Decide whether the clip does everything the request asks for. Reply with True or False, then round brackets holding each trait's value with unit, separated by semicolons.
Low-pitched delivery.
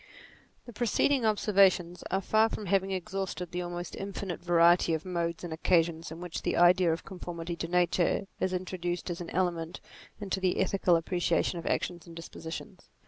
False (180 Hz)